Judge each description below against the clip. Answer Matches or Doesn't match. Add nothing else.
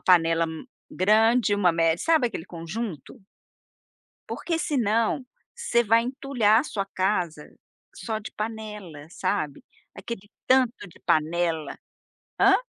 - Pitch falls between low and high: Doesn't match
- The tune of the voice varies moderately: Doesn't match